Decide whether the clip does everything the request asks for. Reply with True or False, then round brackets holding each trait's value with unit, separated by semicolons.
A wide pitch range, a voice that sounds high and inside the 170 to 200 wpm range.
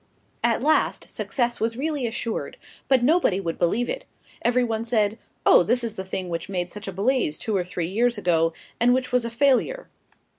False (4.7 semitones; 230 Hz; 195 wpm)